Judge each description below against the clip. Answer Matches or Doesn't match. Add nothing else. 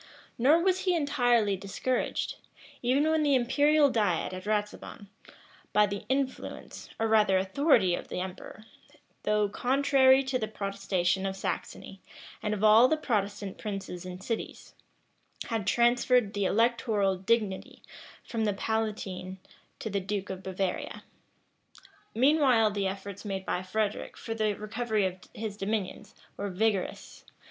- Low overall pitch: Doesn't match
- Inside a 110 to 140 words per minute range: Matches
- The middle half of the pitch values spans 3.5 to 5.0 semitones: Matches